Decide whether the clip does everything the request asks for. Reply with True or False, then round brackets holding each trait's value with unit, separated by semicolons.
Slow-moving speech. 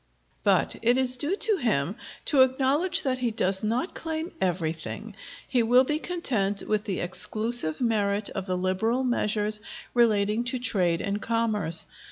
False (155 wpm)